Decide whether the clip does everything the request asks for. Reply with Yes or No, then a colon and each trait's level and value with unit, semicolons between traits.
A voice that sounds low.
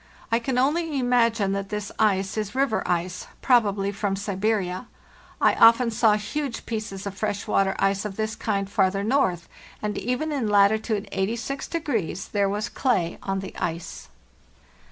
No: high, 210 Hz